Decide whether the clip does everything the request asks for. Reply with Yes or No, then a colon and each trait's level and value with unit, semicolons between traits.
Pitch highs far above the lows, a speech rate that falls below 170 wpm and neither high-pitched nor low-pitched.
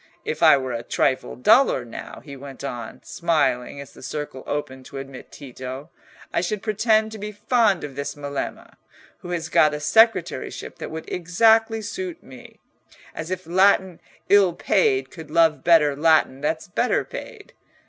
Yes: wide, 7.0 semitones; average, 160 wpm; medium, 160 Hz